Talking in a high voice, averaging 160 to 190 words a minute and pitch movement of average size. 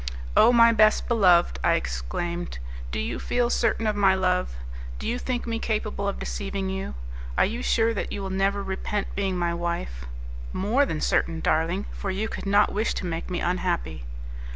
Yes: high, 195 Hz; average, 185 wpm; average, 3.9 semitones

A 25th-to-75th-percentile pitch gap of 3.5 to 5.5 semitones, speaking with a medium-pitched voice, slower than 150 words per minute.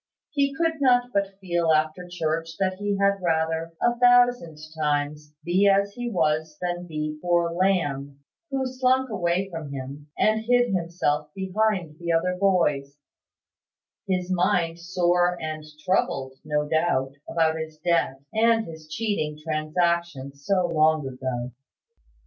Yes: average, 4.2 semitones; medium, 170 Hz; slow, 135 wpm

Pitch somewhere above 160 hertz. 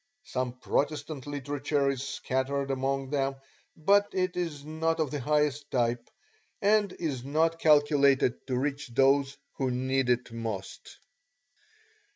No: medium, 140 Hz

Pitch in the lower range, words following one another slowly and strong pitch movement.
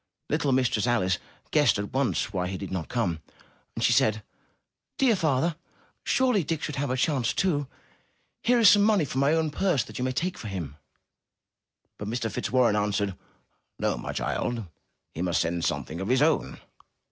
No: low, 125 Hz; average, 180 wpm; wide, 7.4 semitones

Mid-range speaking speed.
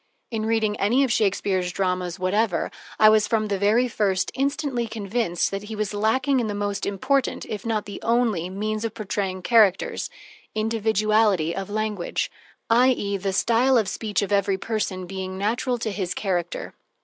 Yes: average, 165 wpm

